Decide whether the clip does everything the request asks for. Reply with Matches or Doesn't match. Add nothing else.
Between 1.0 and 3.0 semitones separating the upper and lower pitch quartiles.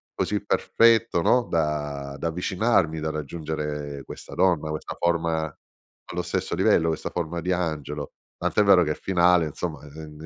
Matches